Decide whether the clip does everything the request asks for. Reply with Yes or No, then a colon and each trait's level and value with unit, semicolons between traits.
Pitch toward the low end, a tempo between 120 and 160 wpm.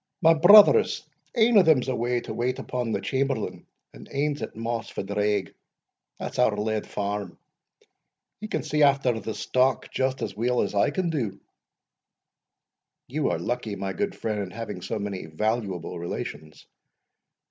Yes: low, 120 Hz; average, 155 wpm